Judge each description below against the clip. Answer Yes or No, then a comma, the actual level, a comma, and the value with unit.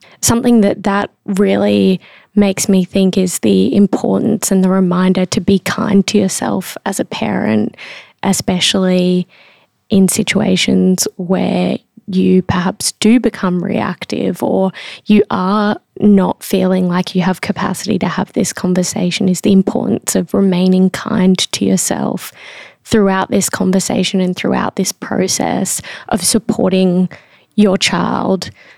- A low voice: No, high, 190 Hz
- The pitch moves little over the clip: Yes, narrow, 2.1 semitones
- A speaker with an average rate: No, slow, 130 wpm